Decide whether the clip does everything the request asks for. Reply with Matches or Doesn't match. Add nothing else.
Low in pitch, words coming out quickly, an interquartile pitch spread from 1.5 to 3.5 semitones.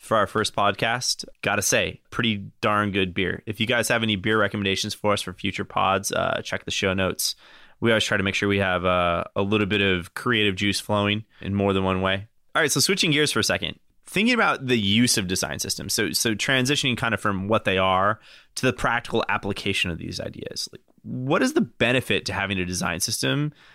Matches